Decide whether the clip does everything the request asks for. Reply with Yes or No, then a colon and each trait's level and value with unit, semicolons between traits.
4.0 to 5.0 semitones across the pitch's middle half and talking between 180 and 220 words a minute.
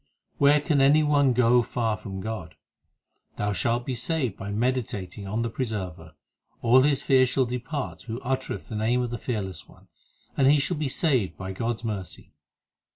Yes: average, 4.3 semitones; average, 185 wpm